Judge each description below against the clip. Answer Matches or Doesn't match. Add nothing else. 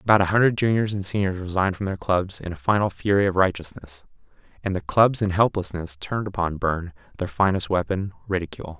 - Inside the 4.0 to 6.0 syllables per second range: Doesn't match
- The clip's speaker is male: Matches